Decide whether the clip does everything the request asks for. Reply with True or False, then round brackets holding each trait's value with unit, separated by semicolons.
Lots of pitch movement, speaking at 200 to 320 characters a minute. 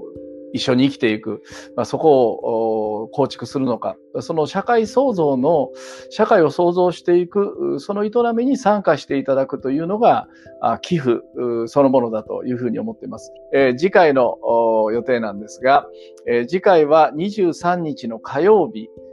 True (7.7 semitones; 295 characters per minute)